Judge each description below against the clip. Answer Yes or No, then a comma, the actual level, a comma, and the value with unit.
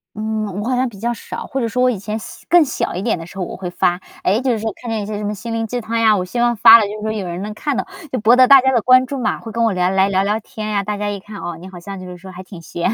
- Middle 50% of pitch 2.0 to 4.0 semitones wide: Yes, average, 3.6 semitones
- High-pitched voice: Yes, high, 215 Hz